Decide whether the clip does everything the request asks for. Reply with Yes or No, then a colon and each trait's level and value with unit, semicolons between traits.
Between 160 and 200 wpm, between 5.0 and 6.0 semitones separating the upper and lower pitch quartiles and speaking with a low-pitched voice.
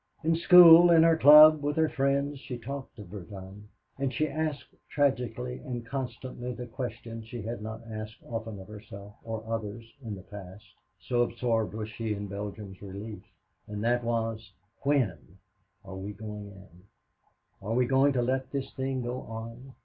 No: average, 170 wpm; average, 4.1 semitones; low, 115 Hz